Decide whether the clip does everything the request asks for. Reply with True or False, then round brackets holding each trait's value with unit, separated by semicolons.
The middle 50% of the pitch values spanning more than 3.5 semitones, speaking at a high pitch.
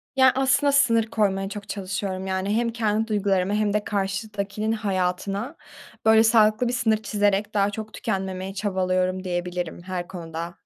False (2.7 semitones; 205 Hz)